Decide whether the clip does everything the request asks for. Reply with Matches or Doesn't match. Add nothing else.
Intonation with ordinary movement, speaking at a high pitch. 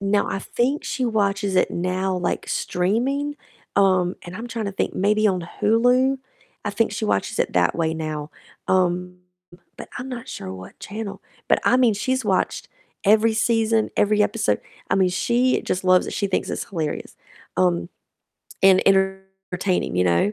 Matches